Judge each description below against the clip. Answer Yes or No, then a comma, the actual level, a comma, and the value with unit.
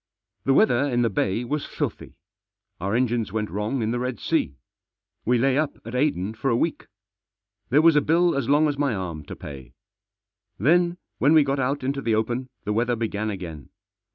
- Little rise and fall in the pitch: No, average, 4.6 semitones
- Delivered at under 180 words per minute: No, average, 195 wpm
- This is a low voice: Yes, low, 125 Hz